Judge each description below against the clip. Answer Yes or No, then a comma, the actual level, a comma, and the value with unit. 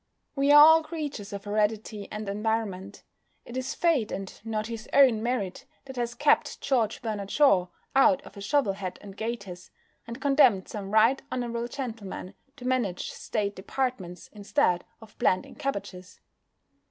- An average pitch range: Yes, average, 4.8 semitones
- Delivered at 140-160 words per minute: Yes, average, 155 wpm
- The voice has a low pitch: No, high, 220 Hz